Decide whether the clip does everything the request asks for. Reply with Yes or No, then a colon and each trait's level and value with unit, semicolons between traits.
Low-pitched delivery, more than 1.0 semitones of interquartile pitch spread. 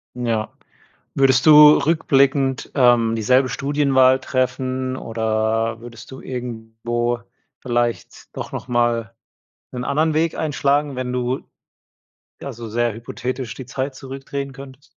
Yes: low, 130 Hz; narrow, 2.5 semitones